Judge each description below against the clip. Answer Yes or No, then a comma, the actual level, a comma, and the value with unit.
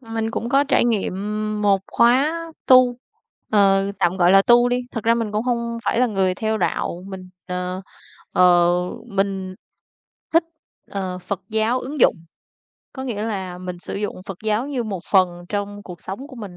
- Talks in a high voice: Yes, high, 205 Hz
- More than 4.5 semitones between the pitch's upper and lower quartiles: No, average, 4.0 semitones